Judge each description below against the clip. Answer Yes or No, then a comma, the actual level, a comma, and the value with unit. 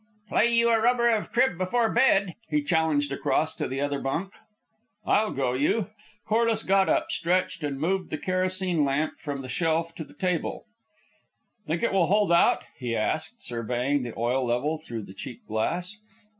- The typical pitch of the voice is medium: Yes, medium, 165 Hz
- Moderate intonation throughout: No, wide, 6.9 semitones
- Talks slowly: No, average, 175 wpm